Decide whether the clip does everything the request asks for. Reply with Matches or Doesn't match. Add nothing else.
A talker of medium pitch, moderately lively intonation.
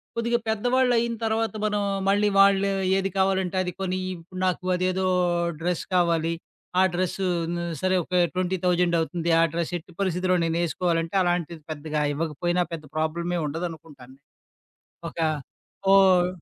Doesn't match